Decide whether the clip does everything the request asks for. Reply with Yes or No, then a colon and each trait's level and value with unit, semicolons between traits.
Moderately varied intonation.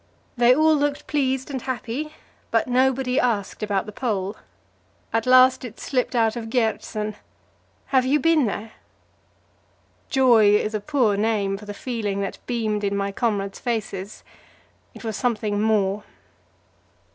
Yes: average, 3.8 semitones